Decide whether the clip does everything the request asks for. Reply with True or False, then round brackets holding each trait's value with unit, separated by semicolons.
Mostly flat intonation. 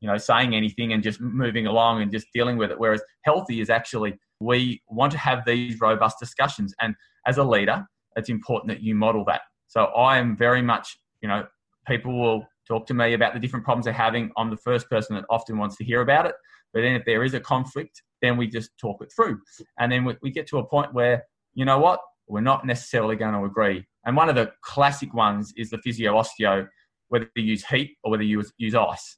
True (2.1 semitones)